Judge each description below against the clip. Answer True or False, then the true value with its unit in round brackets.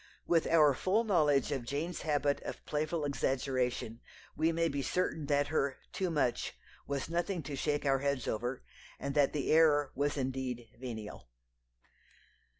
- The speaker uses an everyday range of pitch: True (3.0 semitones)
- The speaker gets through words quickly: False (150 wpm)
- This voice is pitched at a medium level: True (145 Hz)